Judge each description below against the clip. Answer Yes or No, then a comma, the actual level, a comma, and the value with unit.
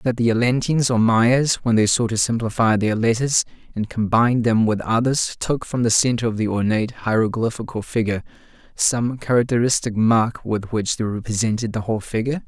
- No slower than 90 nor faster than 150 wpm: No, average, 175 wpm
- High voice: No, low, 115 Hz